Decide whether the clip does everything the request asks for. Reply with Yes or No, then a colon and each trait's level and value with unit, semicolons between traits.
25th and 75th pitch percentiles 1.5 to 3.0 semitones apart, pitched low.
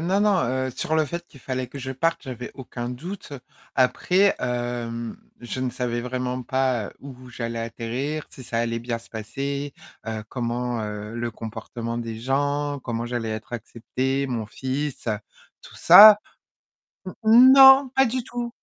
No: average, 3.5 semitones; low, 125 Hz